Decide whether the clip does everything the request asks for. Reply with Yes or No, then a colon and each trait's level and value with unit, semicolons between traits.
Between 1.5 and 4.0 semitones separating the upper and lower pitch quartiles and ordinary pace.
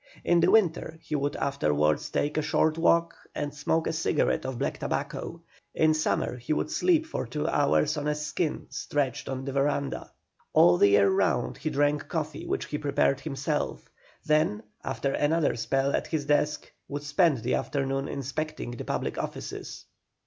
Yes: narrow, 2.4 semitones; average, 170 wpm